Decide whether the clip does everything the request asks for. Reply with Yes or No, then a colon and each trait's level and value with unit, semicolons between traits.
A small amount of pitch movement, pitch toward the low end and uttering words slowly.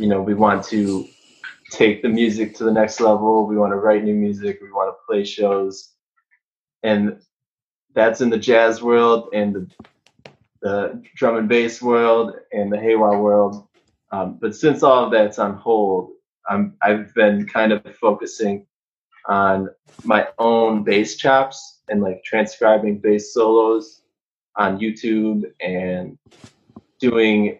No: narrow, 1.9 semitones; low, 110 Hz; average, 150 wpm